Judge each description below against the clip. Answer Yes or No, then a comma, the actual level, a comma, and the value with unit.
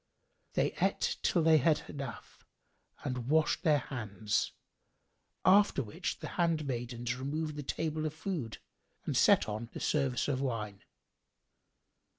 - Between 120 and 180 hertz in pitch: Yes, medium, 140 Hz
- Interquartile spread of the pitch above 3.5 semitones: Yes, average, 4.5 semitones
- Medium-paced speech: No, slow, 130 wpm